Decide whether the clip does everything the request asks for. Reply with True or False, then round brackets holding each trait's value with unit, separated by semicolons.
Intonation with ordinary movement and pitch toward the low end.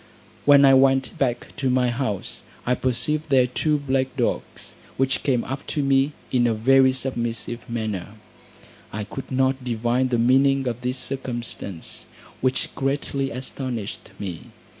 False (2.1 semitones; 130 Hz)